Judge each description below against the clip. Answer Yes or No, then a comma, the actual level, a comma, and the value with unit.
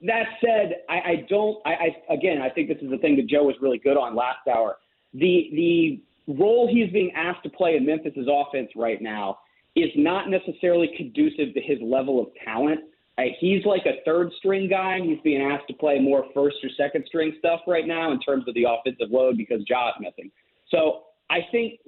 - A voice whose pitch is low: No, medium, 160 Hz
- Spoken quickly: Yes, fast, 210 wpm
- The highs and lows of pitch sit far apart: Yes, wide, 5.9 semitones